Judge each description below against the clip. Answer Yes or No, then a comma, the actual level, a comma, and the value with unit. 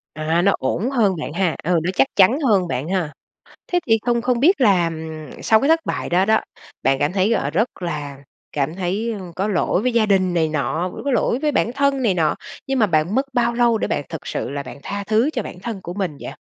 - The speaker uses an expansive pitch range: Yes, wide, 6.2 semitones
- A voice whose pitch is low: No, high, 195 Hz